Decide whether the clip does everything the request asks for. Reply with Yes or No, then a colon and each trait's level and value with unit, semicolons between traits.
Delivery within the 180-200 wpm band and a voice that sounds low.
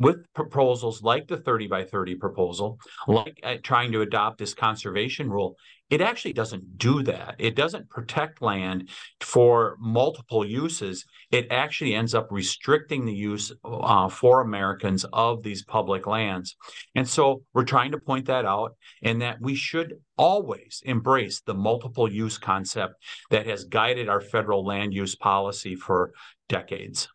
No: average, 155 wpm; low, 115 Hz